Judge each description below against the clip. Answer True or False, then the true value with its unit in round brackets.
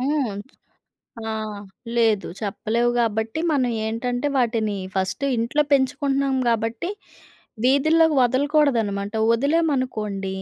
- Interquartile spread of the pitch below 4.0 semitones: False (4.3 semitones)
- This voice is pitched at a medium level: False (240 Hz)